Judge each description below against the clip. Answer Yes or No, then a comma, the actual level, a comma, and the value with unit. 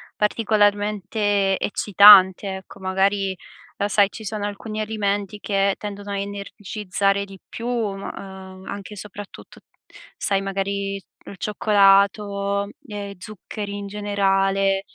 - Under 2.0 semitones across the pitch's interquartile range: Yes, narrow, 1.0 semitones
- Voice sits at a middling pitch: No, high, 200 Hz